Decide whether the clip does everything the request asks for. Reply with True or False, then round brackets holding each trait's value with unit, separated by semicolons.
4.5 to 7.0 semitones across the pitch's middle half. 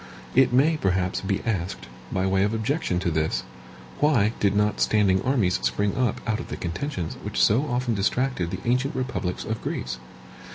True (5.2 semitones)